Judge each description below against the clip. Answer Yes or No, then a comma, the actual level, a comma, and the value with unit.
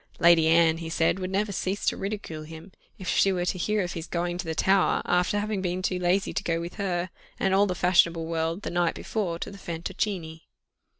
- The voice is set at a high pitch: No, medium, 180 Hz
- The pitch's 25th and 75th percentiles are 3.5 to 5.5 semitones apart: No, narrow, 2.5 semitones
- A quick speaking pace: Yes, fast, 225 wpm